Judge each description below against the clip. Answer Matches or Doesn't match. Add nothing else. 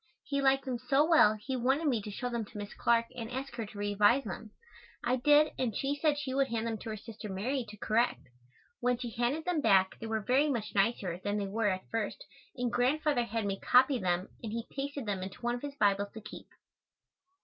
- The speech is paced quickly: Matches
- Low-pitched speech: Doesn't match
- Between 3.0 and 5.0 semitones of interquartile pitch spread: Matches